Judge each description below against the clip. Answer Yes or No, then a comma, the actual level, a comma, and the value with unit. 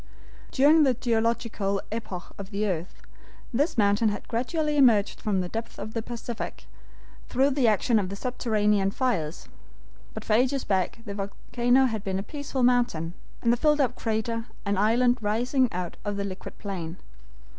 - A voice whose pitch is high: Yes, high, 225 Hz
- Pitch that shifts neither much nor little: Yes, average, 3.8 semitones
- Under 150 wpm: No, average, 165 wpm